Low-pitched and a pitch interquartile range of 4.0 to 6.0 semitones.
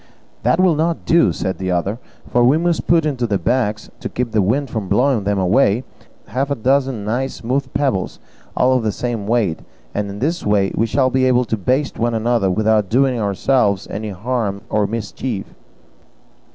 Yes: low, 115 Hz; average, 4.4 semitones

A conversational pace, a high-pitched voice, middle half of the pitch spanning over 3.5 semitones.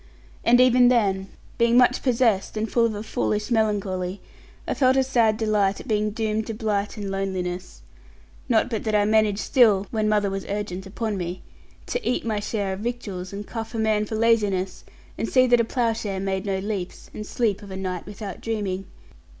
No: average, 195 wpm; high, 210 Hz; average, 2.7 semitones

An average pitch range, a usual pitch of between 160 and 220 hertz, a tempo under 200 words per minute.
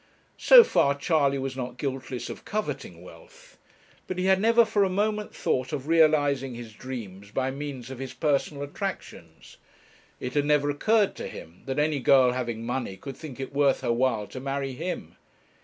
No: average, 4.1 semitones; medium, 140 Hz; average, 180 wpm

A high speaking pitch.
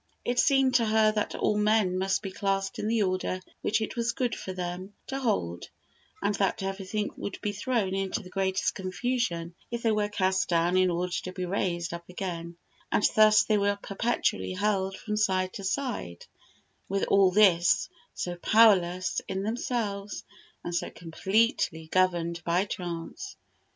Yes: high, 195 Hz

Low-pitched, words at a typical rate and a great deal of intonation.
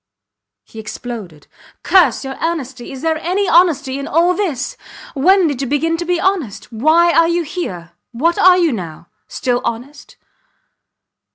No: very high, 295 Hz; average, 155 wpm; wide, 5.9 semitones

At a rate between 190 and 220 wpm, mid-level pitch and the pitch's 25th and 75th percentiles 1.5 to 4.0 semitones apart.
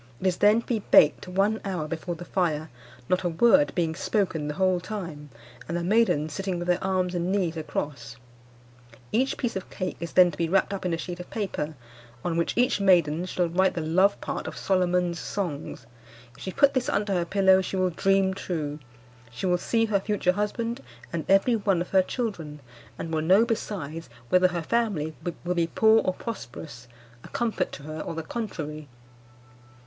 Yes: average, 195 wpm; medium, 180 Hz; average, 3.4 semitones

